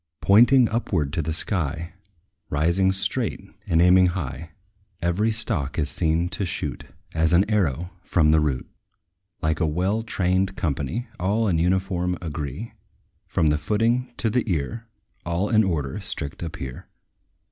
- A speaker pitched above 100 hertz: No, very low, 90 Hz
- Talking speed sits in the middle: Yes, average, 145 wpm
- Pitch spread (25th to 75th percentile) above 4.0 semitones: Yes, average, 4.5 semitones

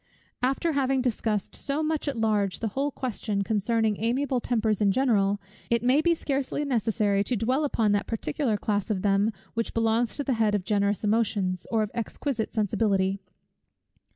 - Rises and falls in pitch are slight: No, average, 3.9 semitones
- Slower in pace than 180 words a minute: Yes, average, 170 wpm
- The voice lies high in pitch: Yes, high, 225 Hz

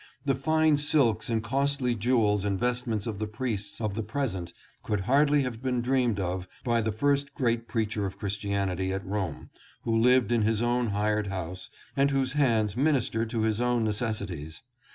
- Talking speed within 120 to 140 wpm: No, average, 180 wpm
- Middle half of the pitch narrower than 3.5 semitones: No, average, 3.8 semitones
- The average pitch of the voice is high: No, low, 115 Hz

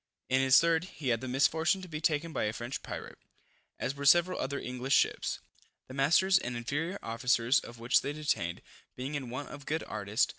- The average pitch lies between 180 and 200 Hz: No, low, 135 Hz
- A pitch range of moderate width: Yes, average, 4.5 semitones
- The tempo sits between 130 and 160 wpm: No, average, 200 wpm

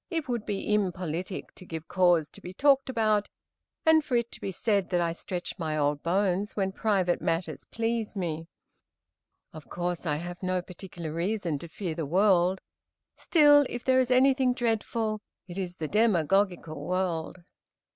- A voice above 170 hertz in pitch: Yes, medium, 185 Hz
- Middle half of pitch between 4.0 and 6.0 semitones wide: Yes, average, 4.5 semitones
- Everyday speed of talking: Yes, average, 165 wpm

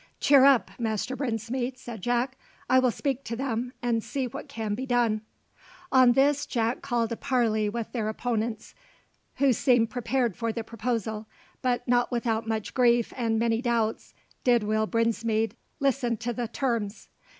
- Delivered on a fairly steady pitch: Yes, narrow, 2.2 semitones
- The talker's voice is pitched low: No, high, 235 Hz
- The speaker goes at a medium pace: Yes, average, 160 wpm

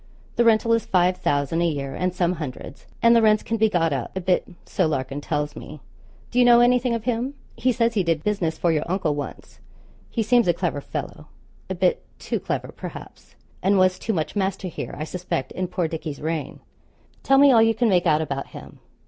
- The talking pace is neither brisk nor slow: No, fast, 215 wpm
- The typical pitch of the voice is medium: Yes, medium, 180 Hz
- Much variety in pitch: Yes, wide, 6.3 semitones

